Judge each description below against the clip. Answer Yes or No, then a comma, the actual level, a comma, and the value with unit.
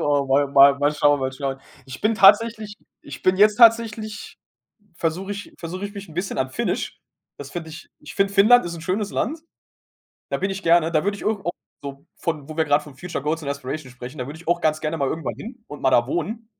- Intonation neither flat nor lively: No, wide, 5.9 semitones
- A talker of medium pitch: Yes, medium, 165 Hz